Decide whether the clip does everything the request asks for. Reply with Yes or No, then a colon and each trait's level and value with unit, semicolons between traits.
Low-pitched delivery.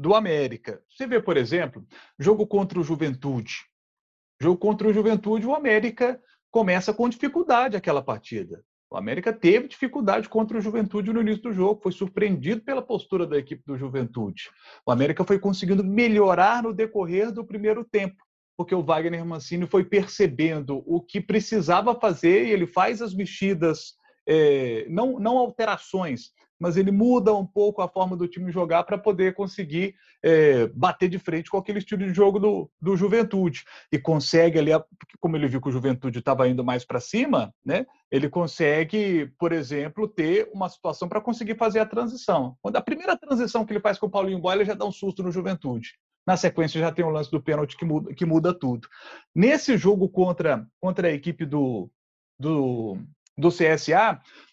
No: high, 190 Hz